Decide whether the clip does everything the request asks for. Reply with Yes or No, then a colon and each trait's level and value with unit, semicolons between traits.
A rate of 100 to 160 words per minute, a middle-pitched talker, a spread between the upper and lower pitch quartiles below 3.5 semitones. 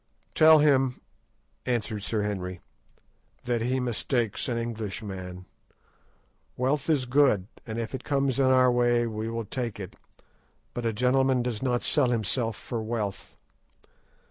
No: average, 140 wpm; low, 120 Hz; average, 3.1 semitones